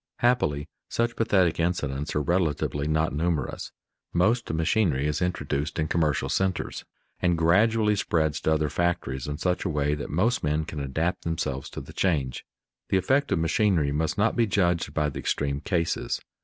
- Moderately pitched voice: No, very low, 80 Hz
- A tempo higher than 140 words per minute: Yes, average, 170 wpm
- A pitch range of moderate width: Yes, average, 4.1 semitones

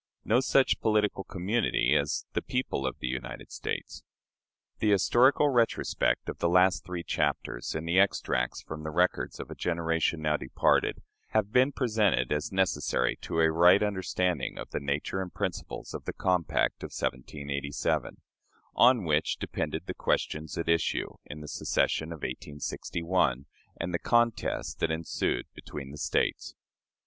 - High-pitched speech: No, very low, 85 Hz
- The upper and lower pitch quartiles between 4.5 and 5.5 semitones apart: Yes, average, 5.0 semitones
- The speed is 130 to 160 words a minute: Yes, average, 155 wpm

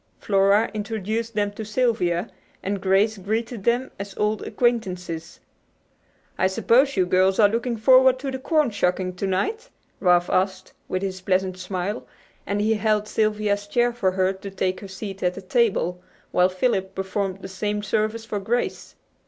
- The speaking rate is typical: Yes, average, 165 wpm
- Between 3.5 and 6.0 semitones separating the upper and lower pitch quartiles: No, average, 3.0 semitones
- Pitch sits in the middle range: No, high, 205 Hz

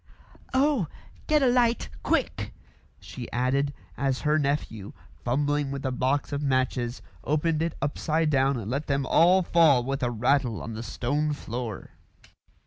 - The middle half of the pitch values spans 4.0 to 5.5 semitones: No, average, 3.3 semitones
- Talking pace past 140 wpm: Yes, average, 155 wpm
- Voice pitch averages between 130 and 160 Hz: Yes, medium, 140 Hz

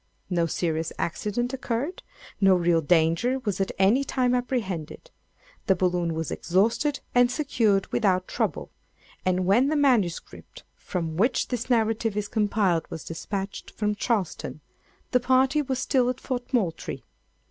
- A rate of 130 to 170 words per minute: Yes, average, 140 wpm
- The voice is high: Yes, high, 210 Hz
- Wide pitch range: Yes, wide, 5.8 semitones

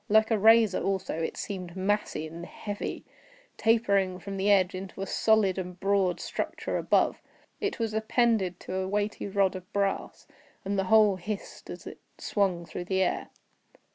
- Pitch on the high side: Yes, high, 195 Hz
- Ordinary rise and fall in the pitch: No, narrow, 2.3 semitones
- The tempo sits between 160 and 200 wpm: Yes, average, 170 wpm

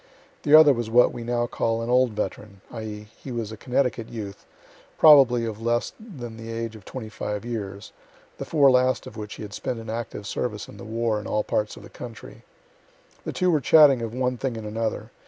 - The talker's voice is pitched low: Yes, low, 115 Hz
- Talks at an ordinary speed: No, fast, 215 wpm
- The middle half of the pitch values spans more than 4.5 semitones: No, average, 2.7 semitones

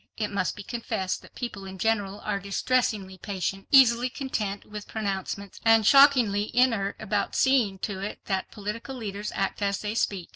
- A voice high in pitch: Yes, high, 210 Hz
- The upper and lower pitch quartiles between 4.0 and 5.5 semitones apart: No, average, 2.8 semitones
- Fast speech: No, average, 170 wpm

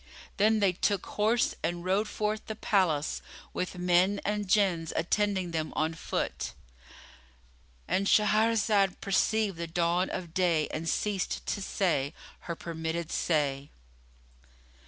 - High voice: No, medium, 180 Hz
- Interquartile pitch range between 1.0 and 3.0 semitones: No, average, 4.1 semitones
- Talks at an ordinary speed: No, slow, 120 wpm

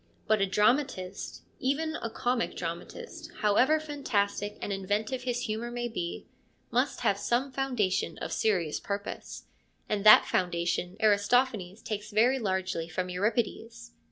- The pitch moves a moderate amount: Yes, average, 4.3 semitones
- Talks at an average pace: No, slow, 130 wpm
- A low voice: No, high, 215 Hz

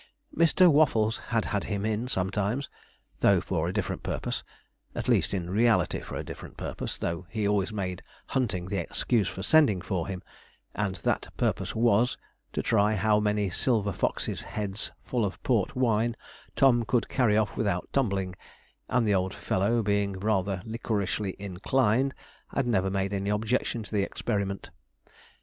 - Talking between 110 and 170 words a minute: Yes, average, 160 wpm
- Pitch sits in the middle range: No, low, 105 Hz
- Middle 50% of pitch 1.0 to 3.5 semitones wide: Yes, average, 3.1 semitones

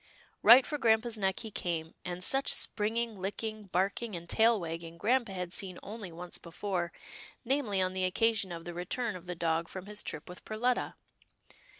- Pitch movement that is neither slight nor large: Yes, average, 4.3 semitones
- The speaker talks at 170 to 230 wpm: Yes, average, 185 wpm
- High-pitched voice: Yes, high, 195 Hz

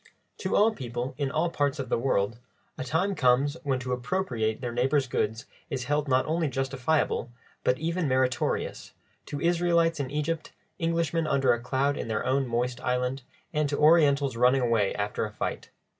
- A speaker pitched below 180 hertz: Yes, low, 135 Hz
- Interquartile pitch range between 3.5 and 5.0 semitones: Yes, average, 3.9 semitones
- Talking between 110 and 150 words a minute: No, average, 175 wpm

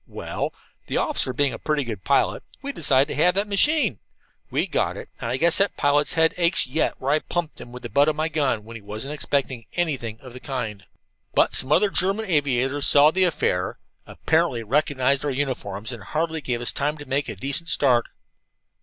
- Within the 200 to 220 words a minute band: Yes, fast, 205 wpm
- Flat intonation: No, average, 4.2 semitones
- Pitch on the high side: No, medium, 140 Hz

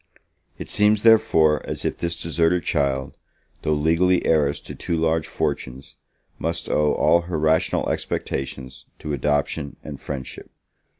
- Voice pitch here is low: Yes, very low, 80 Hz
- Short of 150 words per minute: Yes, slow, 135 wpm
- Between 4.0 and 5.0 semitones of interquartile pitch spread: No, average, 2.8 semitones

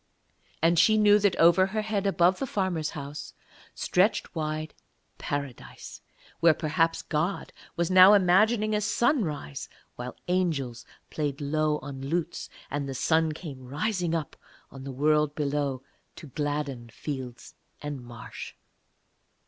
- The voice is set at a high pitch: No, medium, 155 Hz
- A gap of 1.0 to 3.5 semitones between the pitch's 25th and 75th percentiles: No, average, 4.7 semitones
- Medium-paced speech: No, slow, 130 wpm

